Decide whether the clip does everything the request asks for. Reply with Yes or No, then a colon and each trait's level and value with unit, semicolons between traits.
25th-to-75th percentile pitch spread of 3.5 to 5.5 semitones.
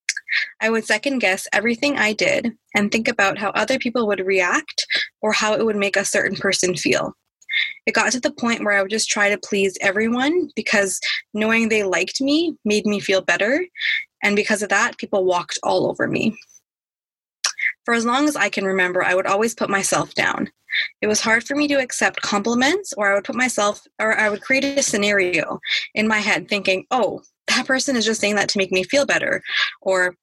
Yes: average, 4.8 semitones